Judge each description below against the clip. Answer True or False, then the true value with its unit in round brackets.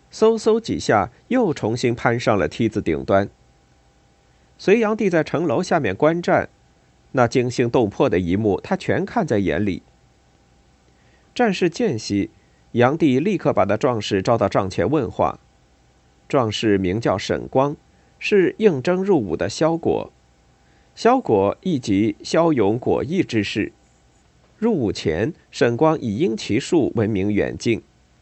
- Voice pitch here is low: True (105 Hz)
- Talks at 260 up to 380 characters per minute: False (200 characters per minute)